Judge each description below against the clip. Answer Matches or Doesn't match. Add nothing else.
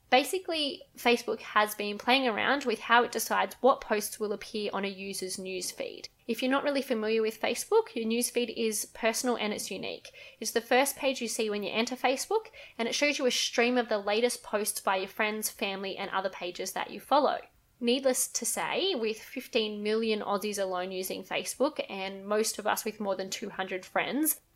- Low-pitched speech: Doesn't match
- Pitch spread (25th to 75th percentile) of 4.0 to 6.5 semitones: Doesn't match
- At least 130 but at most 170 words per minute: Doesn't match